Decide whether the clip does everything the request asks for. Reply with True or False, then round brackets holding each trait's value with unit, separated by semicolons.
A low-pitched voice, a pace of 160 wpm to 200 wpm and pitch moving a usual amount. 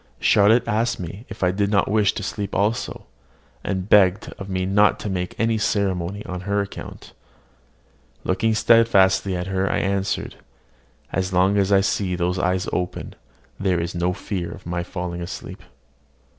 False (95 Hz; 165 wpm; 2.0 semitones)